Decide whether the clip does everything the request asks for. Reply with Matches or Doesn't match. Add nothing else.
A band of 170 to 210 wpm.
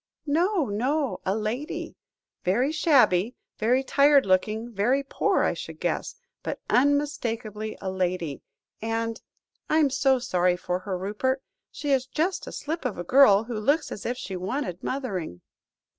Doesn't match